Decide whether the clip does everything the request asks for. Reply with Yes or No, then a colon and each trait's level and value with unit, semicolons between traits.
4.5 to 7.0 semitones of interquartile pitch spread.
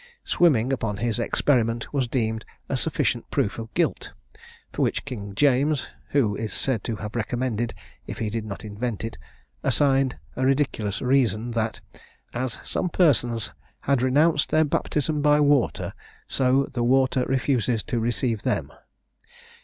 No: average, 3.5 semitones